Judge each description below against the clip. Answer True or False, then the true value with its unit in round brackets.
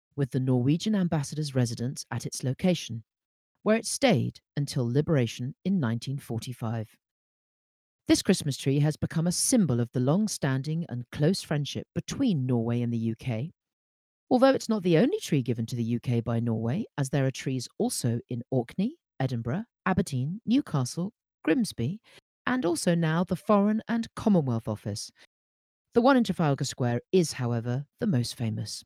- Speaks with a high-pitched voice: False (140 Hz)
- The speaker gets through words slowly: False (155 wpm)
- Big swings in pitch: True (7.6 semitones)